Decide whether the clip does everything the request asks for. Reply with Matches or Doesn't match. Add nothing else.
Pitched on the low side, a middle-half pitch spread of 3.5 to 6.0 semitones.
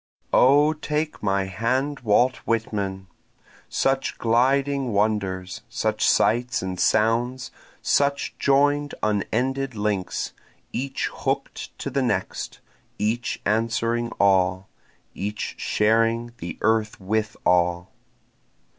Matches